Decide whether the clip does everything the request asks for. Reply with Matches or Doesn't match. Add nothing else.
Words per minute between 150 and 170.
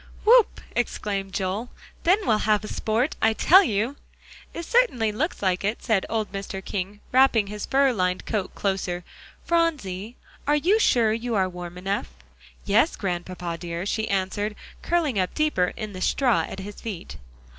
Matches